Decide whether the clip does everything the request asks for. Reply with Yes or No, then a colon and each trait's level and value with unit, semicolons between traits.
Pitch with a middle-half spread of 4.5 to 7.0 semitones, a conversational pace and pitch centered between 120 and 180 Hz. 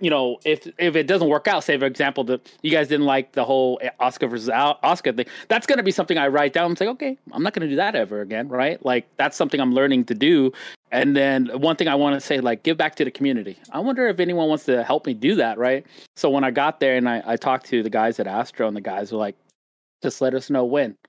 No: average, 4.8 semitones; fast, 280 wpm; medium, 140 Hz